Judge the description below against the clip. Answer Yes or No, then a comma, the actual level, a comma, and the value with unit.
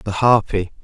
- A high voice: No, low, 100 Hz